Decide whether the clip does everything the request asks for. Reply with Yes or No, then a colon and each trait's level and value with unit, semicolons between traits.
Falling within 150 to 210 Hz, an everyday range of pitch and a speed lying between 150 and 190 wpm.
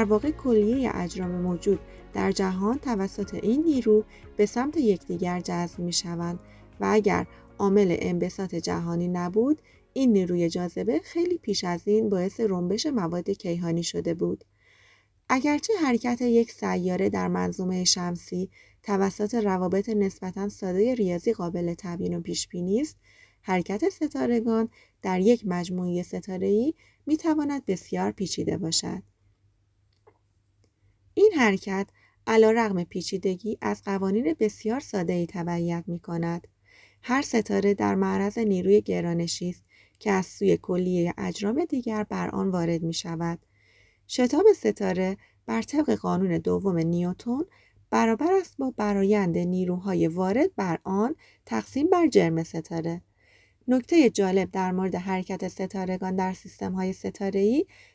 No: high, 190 Hz; average, 3.9 semitones; average, 130 wpm